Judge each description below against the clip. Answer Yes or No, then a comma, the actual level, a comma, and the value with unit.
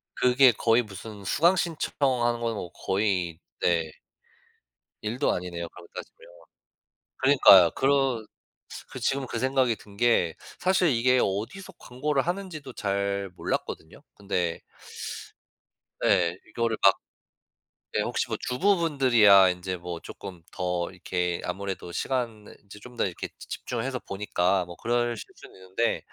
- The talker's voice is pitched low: Yes, low, 110 Hz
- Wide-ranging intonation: Yes, wide, 5.8 semitones